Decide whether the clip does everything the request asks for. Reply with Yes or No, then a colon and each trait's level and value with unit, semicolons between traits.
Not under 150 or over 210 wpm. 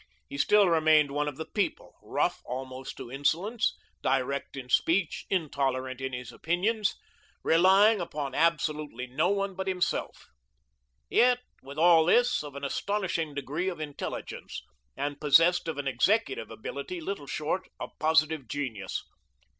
No: average, 140 wpm